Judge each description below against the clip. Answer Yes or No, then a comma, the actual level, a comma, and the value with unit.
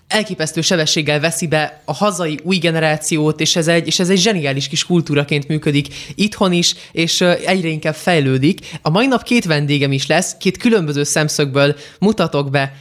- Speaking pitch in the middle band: Yes, medium, 160 Hz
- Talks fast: Yes, fast, 170 wpm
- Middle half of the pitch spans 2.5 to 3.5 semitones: Yes, average, 3.2 semitones